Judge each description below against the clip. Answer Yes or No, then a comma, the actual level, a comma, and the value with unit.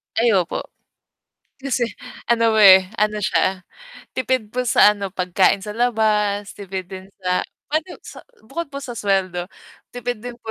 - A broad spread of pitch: No, average, 4.1 semitones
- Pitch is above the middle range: Yes, high, 210 Hz